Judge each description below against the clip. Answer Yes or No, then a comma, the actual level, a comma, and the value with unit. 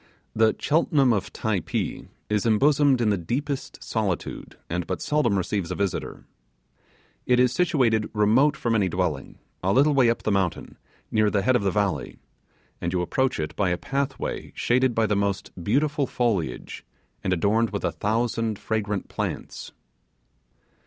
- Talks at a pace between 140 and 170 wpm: Yes, average, 160 wpm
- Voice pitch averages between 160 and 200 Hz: No, low, 110 Hz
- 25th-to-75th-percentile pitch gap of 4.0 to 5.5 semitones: Yes, average, 4.6 semitones